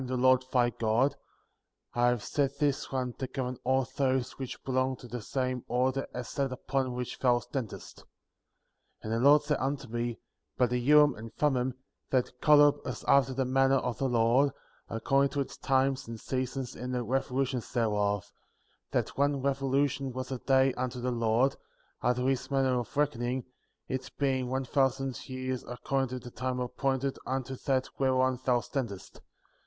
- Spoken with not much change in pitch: Yes, narrow, 1.6 semitones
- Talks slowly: No, average, 175 wpm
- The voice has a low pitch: Yes, low, 130 Hz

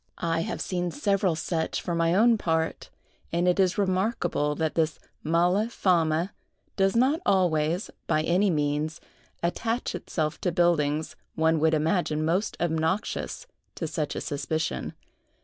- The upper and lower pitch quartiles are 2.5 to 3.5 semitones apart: Yes, average, 3.1 semitones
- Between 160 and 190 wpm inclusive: No, average, 140 wpm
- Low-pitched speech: No, medium, 170 Hz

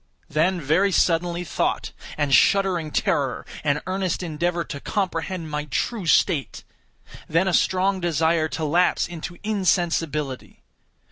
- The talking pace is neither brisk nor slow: No, slow, 125 wpm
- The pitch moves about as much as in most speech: Yes, average, 3.2 semitones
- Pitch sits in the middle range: Yes, medium, 170 Hz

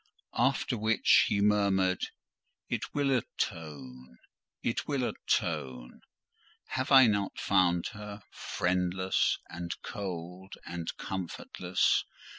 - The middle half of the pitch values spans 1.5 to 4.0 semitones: Yes, average, 3.4 semitones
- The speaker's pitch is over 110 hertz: No, very low, 95 Hz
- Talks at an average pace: No, slow, 90 wpm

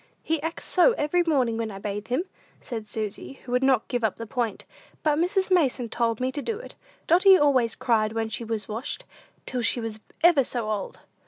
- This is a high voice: Yes, high, 245 Hz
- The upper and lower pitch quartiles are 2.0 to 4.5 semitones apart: No, average, 5.2 semitones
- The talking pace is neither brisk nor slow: No, fast, 210 wpm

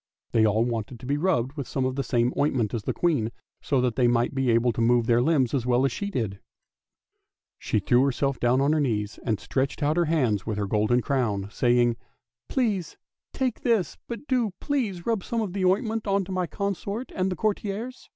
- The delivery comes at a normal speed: No, fast, 220 wpm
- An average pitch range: No, wide, 8.2 semitones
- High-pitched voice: No, low, 135 Hz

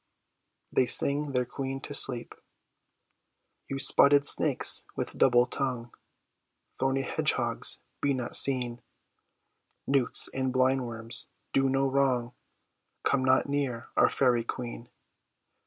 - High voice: No, low, 130 Hz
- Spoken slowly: Yes, slow, 115 wpm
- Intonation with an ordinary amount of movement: No, narrow, 1.9 semitones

